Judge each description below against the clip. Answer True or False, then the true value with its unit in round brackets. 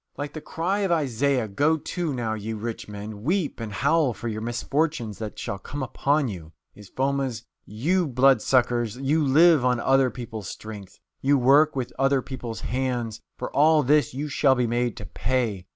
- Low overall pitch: True (130 Hz)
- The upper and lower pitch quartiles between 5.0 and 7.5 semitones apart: False (4.3 semitones)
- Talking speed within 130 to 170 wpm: False (185 wpm)